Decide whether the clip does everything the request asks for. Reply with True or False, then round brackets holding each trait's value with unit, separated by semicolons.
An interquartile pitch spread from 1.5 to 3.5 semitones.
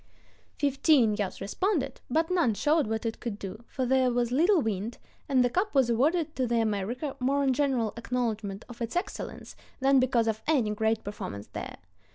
False (4.1 semitones)